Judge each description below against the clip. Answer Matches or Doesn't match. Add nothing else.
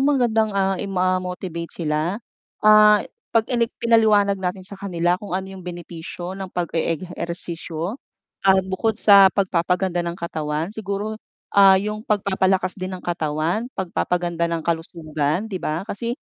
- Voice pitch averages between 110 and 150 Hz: Doesn't match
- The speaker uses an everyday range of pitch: Matches